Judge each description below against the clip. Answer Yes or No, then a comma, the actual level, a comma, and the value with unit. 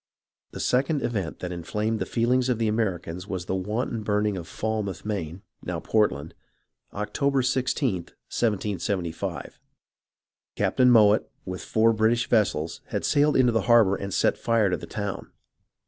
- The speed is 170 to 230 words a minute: No, average, 145 wpm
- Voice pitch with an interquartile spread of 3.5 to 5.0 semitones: Yes, average, 3.8 semitones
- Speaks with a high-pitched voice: No, low, 105 Hz